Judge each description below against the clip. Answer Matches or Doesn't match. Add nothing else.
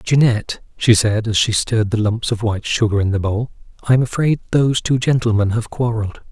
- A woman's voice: Doesn't match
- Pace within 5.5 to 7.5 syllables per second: Matches